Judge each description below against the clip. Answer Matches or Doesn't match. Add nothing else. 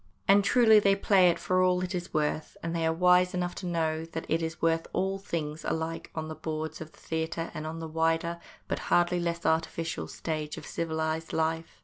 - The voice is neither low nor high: Matches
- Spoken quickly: Matches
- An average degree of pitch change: Doesn't match